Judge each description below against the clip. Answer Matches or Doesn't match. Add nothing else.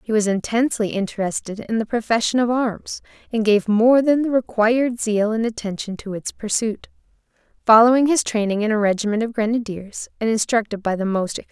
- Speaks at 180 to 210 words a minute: Matches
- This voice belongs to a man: Doesn't match